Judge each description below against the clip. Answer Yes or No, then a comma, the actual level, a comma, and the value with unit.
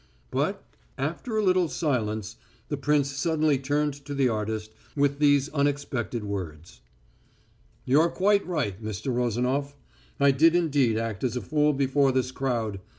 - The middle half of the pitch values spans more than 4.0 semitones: Yes, average, 4.5 semitones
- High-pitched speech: No, low, 135 Hz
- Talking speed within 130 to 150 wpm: Yes, average, 145 wpm